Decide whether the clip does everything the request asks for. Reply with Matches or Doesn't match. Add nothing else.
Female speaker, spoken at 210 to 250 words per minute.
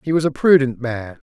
Doesn't match